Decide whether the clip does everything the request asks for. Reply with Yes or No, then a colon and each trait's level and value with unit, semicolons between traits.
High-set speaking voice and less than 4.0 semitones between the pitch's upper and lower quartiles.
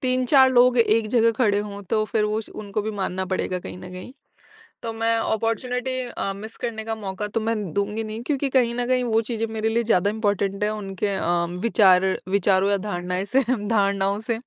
Yes: high, 215 Hz; narrow, 2.5 semitones